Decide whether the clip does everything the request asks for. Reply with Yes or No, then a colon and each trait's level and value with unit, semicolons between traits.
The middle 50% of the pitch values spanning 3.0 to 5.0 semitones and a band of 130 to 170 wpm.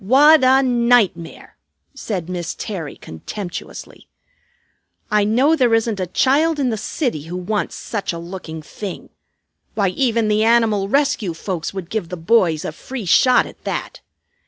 No: wide, 5.5 semitones; average, 155 wpm